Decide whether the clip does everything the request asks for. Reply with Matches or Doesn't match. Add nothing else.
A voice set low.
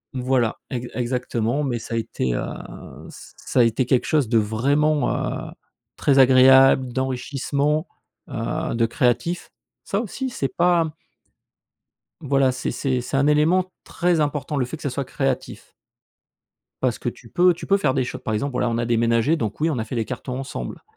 Matches